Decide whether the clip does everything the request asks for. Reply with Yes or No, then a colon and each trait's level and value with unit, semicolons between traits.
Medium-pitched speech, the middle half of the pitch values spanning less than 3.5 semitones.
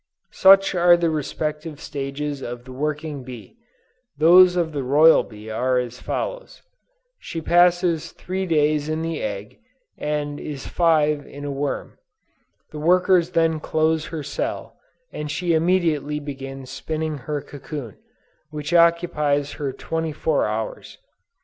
Yes: medium, 150 Hz; average, 2.7 semitones